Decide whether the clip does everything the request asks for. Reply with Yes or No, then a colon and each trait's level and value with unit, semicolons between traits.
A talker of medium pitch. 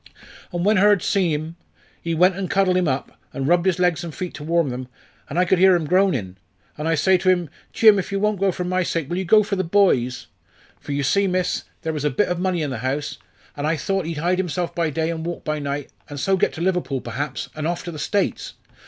Yes: medium, 175 Hz